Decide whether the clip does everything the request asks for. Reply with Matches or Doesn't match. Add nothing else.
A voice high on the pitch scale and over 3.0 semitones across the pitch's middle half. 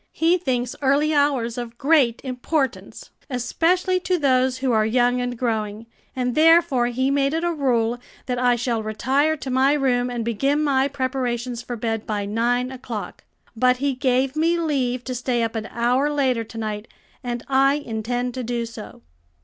Doesn't match